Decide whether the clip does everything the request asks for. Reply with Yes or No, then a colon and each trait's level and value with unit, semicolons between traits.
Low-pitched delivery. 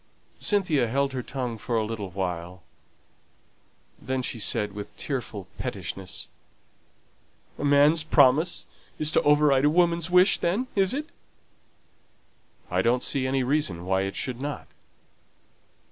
Yes: low, 130 Hz